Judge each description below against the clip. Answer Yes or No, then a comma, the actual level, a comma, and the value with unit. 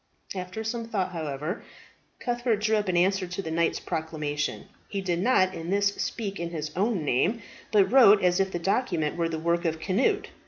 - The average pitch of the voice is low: No, medium, 185 Hz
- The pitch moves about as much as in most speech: Yes, average, 4.1 semitones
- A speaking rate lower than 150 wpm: No, average, 195 wpm